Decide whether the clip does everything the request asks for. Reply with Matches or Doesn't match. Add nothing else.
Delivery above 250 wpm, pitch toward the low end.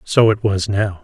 Doesn't match